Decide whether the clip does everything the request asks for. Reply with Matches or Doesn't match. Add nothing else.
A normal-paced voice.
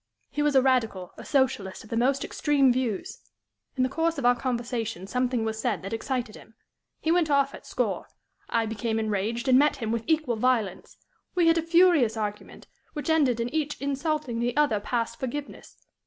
Matches